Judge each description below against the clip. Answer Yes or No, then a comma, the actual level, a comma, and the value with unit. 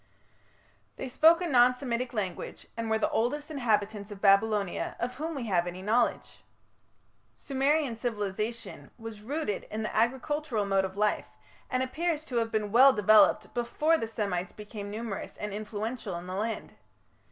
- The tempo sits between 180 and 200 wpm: No, average, 160 wpm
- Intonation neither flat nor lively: Yes, average, 3.7 semitones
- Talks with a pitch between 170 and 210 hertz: No, high, 225 Hz